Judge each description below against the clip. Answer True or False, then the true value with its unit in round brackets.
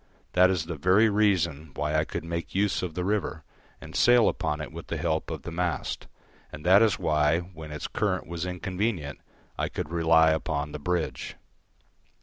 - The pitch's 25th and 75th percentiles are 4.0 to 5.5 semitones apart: False (3.2 semitones)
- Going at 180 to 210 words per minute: True (185 wpm)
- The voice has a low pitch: True (85 Hz)